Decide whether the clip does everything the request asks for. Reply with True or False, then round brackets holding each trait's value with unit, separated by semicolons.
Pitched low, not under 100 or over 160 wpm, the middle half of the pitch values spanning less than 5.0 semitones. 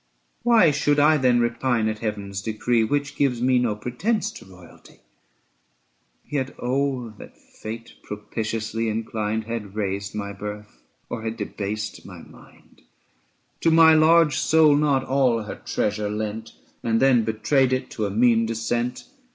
True (115 Hz; 150 wpm; 3.9 semitones)